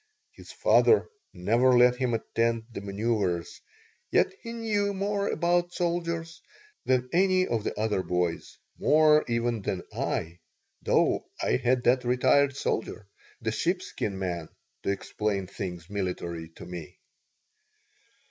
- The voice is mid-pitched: No, low, 115 Hz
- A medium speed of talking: No, slow, 130 wpm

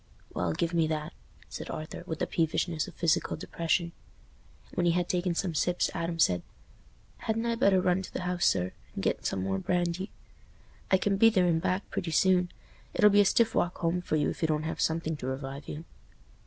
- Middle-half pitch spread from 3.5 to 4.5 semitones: No, average, 2.7 semitones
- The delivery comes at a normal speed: No, fast, 210 wpm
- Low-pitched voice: No, medium, 170 Hz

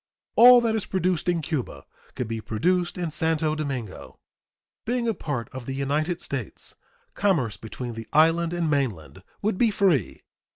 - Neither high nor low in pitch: Yes, medium, 155 Hz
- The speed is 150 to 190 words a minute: Yes, average, 160 wpm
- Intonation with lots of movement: Yes, wide, 6.4 semitones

